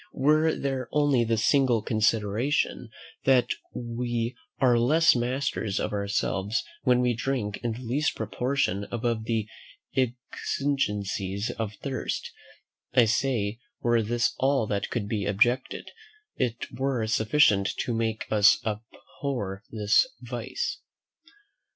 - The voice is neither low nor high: No, low, 120 Hz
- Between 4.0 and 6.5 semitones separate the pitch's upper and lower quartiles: No, average, 3.4 semitones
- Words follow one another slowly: Yes, slow, 120 wpm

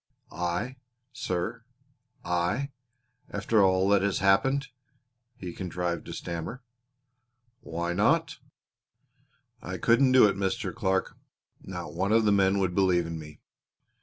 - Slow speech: Yes, slow, 125 wpm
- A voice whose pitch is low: Yes, very low, 95 Hz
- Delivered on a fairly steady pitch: No, average, 4.1 semitones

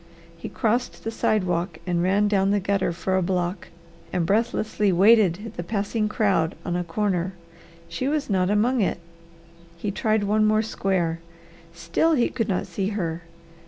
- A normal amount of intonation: Yes, average, 3.4 semitones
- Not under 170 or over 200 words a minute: No, average, 160 wpm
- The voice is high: Yes, high, 200 Hz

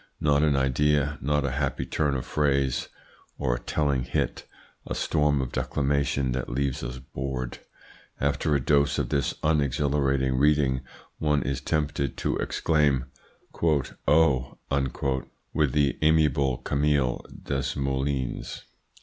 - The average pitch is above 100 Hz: No, very low, 70 Hz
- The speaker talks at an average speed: No, slow, 125 wpm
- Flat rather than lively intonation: Yes, narrow, 1.9 semitones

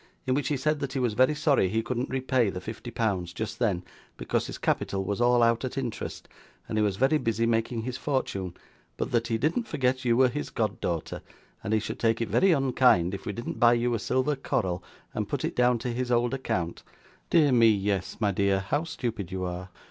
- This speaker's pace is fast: Yes, fast, 225 wpm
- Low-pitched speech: Yes, low, 115 Hz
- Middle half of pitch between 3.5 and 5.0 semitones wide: Yes, average, 4.3 semitones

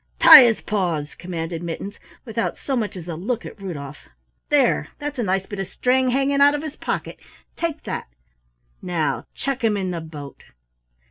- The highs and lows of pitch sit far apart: Yes, wide, 7.5 semitones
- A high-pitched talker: Yes, high, 200 Hz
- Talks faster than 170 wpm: Yes, average, 180 wpm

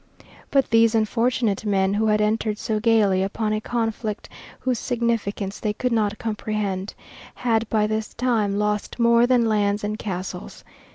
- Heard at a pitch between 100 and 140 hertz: No, high, 215 Hz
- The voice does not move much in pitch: Yes, narrow, 1.9 semitones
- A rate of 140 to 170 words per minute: Yes, average, 155 wpm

